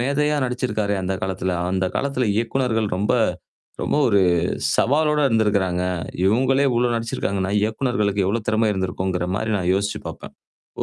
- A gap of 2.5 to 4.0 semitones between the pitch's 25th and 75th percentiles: No, average, 4.6 semitones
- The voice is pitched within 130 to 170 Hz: No, low, 110 Hz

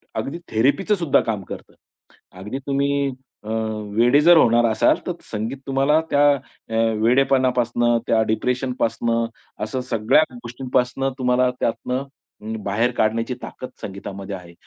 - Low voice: Yes, low, 125 Hz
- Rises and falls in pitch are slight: No, average, 3.3 semitones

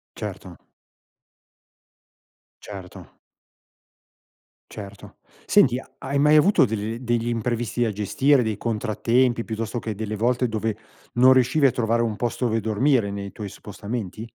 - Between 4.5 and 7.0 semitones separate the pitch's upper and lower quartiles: No, narrow, 2.6 semitones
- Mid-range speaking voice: No, low, 115 Hz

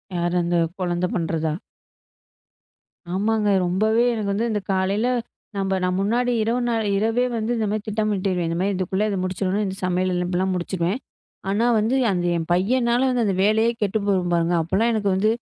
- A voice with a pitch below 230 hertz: Yes, high, 195 Hz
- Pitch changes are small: No, average, 3.1 semitones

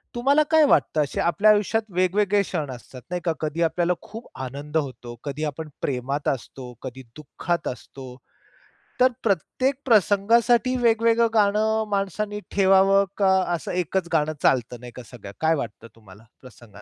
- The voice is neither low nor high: Yes, medium, 175 Hz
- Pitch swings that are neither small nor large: No, wide, 7.5 semitones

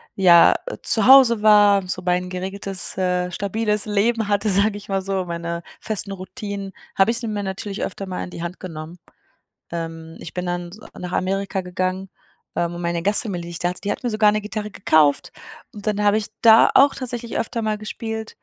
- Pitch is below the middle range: No, high, 195 Hz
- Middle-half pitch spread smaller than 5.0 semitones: Yes, average, 2.9 semitones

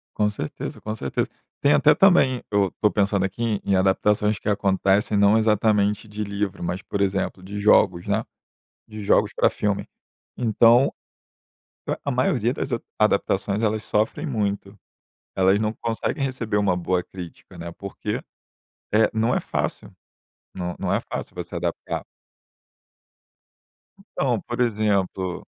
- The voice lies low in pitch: Yes, low, 105 Hz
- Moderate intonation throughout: No, narrow, 2.3 semitones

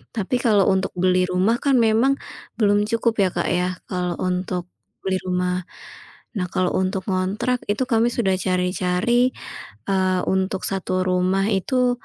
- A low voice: No, high, 190 Hz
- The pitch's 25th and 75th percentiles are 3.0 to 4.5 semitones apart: Yes, average, 3.5 semitones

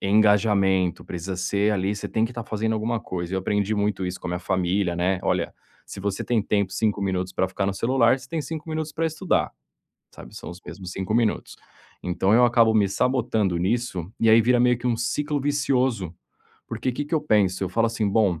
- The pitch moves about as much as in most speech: Yes, average, 4.2 semitones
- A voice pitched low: Yes, low, 105 Hz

